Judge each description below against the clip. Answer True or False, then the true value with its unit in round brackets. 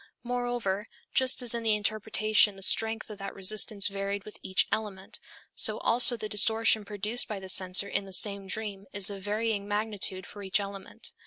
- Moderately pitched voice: False (205 Hz)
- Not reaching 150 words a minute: False (180 wpm)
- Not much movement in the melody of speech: True (1.9 semitones)